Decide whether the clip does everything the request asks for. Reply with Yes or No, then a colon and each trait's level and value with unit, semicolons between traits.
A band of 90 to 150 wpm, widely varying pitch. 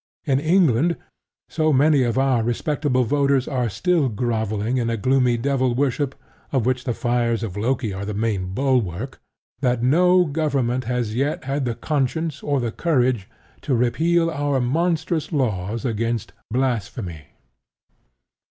No: average, 140 wpm; average, 3.8 semitones